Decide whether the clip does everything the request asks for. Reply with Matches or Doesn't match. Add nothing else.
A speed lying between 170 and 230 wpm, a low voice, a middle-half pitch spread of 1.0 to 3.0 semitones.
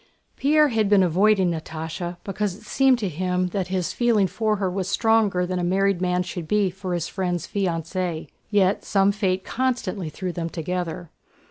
Doesn't match